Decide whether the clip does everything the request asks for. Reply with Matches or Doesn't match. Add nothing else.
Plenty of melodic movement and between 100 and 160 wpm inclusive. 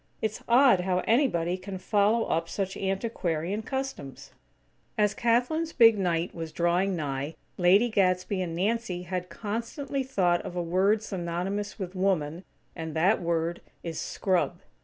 Doesn't match